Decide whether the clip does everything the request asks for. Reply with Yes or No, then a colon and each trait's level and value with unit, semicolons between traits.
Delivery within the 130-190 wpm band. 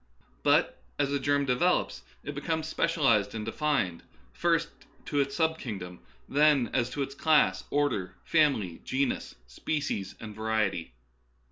Yes: average, 145 wpm